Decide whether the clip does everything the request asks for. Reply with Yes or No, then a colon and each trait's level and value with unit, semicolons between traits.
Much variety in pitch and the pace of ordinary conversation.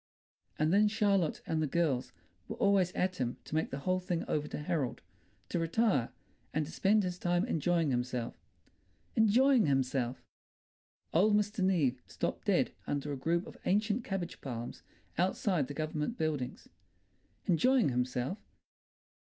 Yes: wide, 6.0 semitones; average, 145 wpm